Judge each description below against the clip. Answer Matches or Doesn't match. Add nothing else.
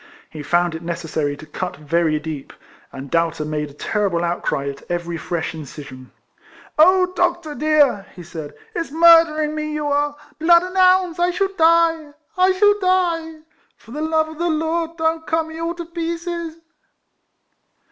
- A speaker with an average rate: Matches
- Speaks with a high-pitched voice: Matches